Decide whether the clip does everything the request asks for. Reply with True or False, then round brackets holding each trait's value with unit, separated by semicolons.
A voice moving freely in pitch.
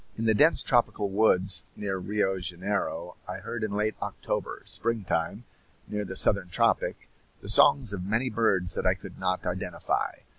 False (3.0 semitones)